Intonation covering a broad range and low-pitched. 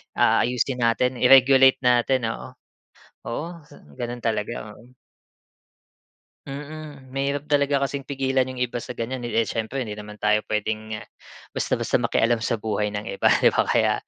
No: average, 3.1 semitones; low, 125 Hz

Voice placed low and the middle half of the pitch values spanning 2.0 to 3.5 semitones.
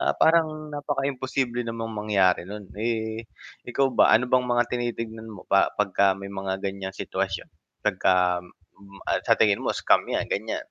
No: low, 110 Hz; average, 3.9 semitones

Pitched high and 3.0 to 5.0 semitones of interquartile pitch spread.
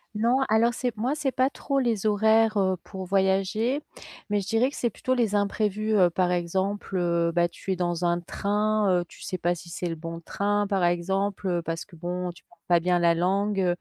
Yes: high, 195 Hz; average, 3.5 semitones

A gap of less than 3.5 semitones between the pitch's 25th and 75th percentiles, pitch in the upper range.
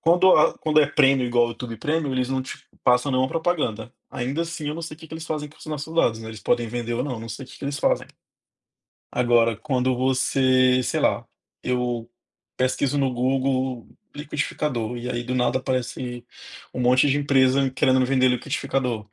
No: average, 2.8 semitones; low, 130 Hz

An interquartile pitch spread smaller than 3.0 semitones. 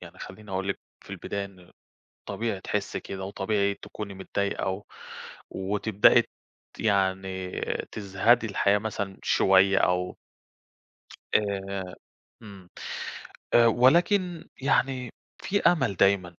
Yes: narrow, 2.4 semitones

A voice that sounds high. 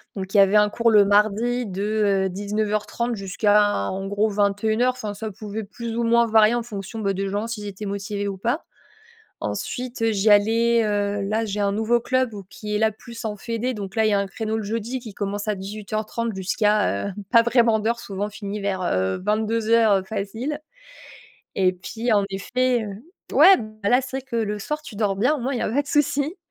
Yes: high, 215 Hz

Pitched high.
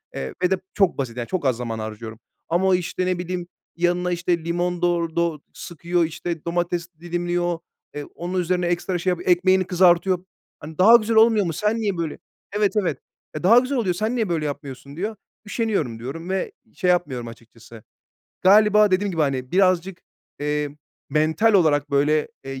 No: medium, 175 Hz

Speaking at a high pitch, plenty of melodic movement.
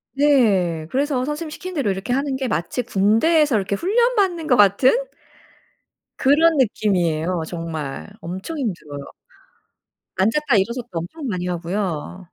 Yes: high, 220 Hz; wide, 8.3 semitones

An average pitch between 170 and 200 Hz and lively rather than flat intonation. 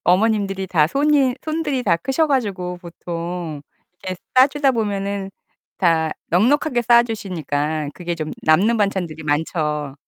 Yes: high, 190 Hz; wide, 6.4 semitones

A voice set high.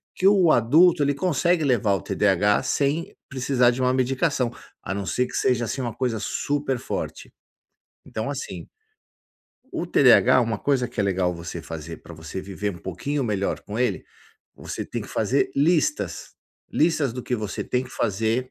No: low, 125 Hz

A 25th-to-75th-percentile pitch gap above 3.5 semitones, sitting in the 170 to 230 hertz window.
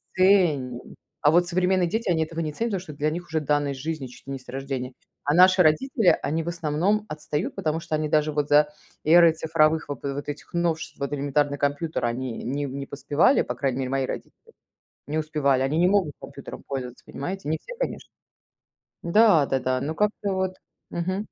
No: average, 3.9 semitones; medium, 155 Hz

